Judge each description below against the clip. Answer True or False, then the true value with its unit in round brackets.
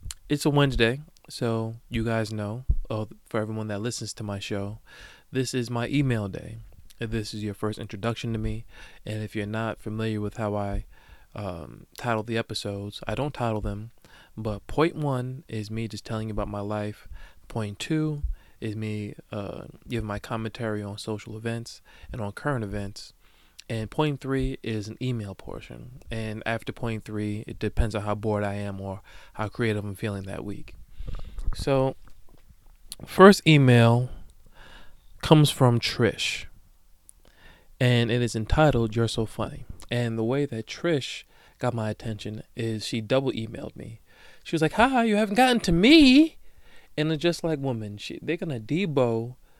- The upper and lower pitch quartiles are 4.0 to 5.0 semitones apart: False (3.4 semitones)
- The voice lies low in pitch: True (110 Hz)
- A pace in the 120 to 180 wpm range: True (165 wpm)